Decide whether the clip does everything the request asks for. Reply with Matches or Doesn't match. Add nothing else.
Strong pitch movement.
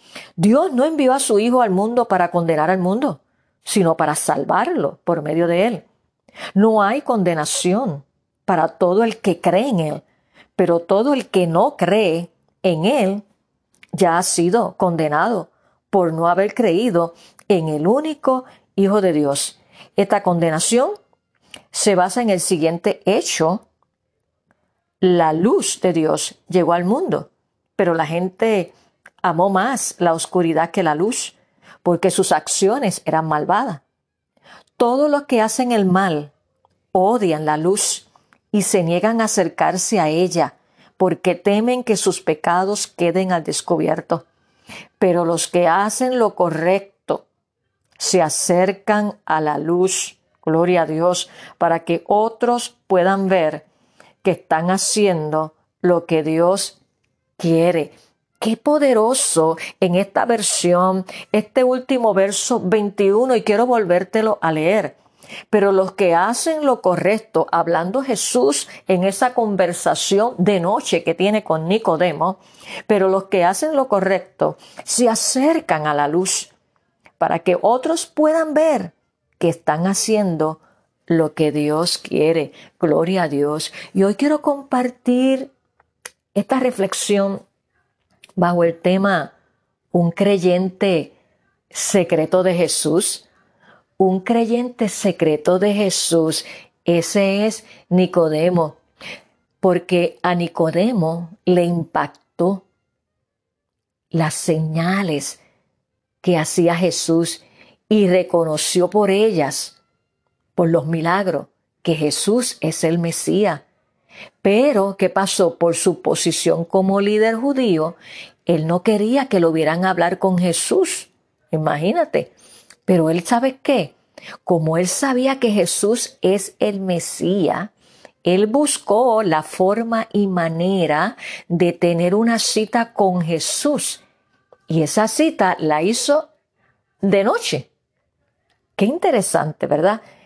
Doesn't match